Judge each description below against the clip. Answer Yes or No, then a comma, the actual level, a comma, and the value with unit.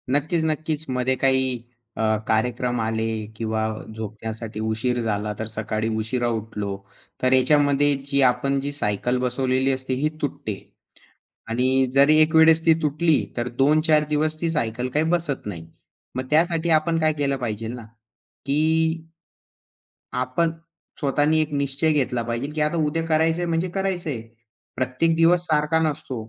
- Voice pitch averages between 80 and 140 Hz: Yes, low, 135 Hz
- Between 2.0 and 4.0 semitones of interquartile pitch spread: No, average, 4.5 semitones